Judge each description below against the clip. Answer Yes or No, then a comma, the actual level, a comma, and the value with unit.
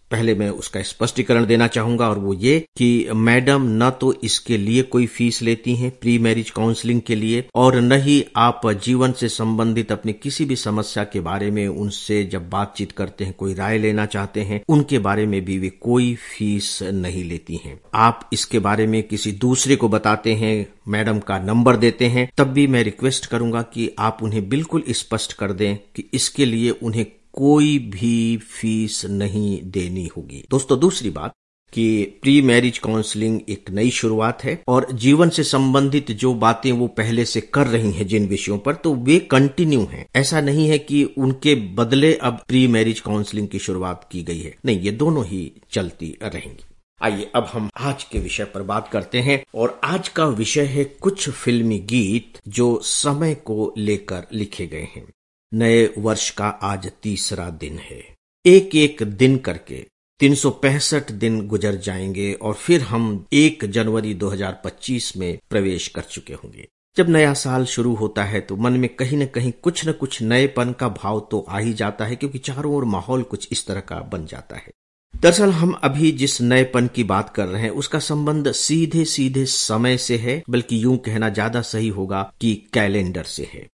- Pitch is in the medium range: No, low, 115 Hz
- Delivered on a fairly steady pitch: No, average, 3.9 semitones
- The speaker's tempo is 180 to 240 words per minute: Yes, average, 185 wpm